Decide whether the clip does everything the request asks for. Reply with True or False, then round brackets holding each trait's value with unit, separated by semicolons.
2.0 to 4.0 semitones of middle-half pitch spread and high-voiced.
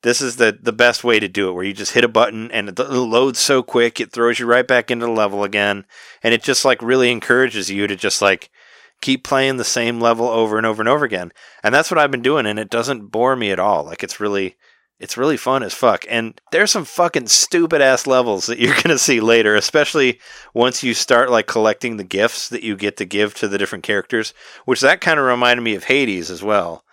False (3.1 semitones; 120 Hz)